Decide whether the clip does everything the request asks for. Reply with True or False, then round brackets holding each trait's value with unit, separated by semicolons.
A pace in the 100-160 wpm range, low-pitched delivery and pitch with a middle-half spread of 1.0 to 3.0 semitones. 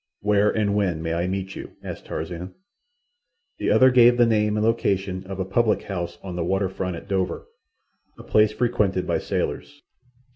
False (175 wpm; 100 Hz; 2.6 semitones)